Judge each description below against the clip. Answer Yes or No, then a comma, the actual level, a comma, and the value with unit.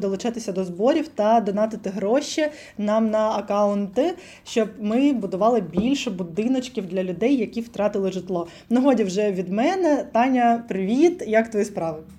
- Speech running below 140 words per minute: No, average, 145 wpm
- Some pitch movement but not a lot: Yes, average, 3.8 semitones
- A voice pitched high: Yes, high, 220 Hz